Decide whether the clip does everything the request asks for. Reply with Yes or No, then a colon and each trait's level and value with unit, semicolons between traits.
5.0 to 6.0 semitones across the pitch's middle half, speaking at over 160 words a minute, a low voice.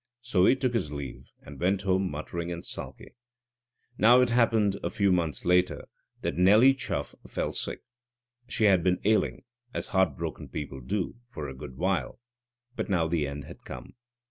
Yes: wide, 5.6 semitones; average, 170 wpm; very low, 90 Hz